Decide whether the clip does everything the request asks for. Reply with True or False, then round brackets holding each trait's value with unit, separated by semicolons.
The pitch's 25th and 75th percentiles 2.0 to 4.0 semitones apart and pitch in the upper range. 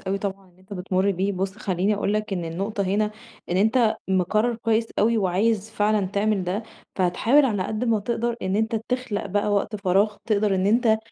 True (2.4 semitones; 205 Hz)